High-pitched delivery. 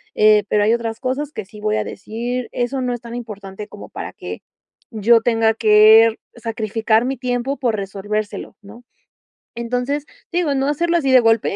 Yes: high, 230 Hz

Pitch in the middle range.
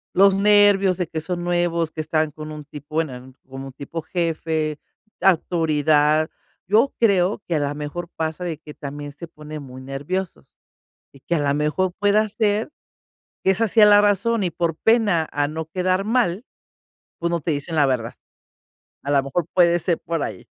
Yes: medium, 165 Hz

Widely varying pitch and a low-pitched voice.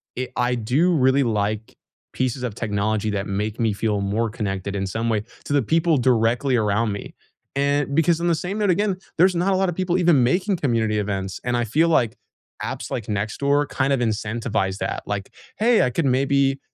Yes: wide, 6.0 semitones; low, 125 Hz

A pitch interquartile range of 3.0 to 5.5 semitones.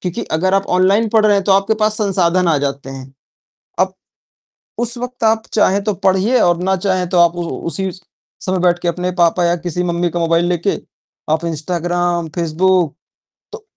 No: narrow, 2.4 semitones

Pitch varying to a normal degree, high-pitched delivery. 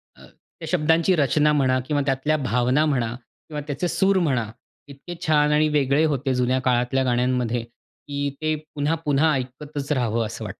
No: average, 3.2 semitones; medium, 140 Hz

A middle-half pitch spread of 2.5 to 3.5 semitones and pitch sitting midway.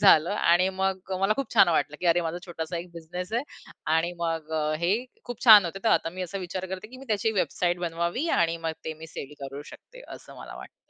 Yes: average, 3.0 semitones; medium, 175 Hz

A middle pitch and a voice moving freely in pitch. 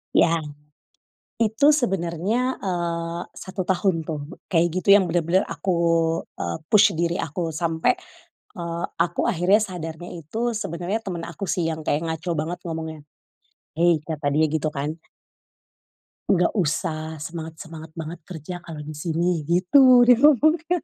No: medium, 170 Hz; average, 2.8 semitones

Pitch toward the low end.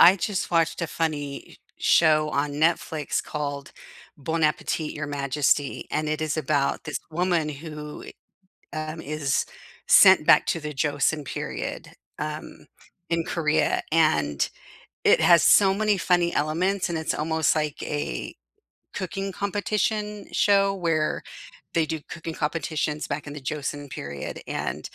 No: medium, 155 Hz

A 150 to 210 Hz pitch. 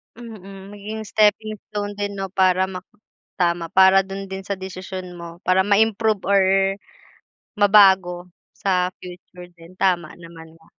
Yes: high, 190 Hz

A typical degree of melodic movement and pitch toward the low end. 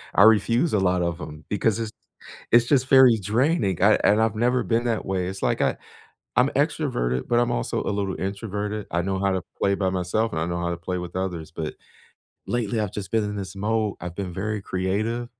Yes: average, 3.5 semitones; low, 100 Hz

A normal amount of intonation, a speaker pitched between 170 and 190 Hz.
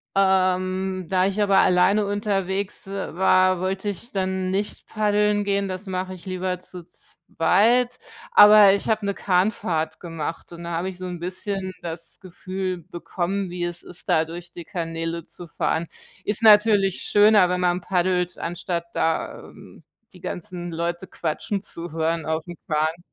No: narrow, 2.3 semitones; medium, 185 Hz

